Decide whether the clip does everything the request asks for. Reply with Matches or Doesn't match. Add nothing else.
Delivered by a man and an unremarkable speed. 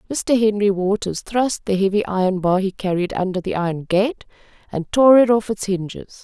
Doesn't match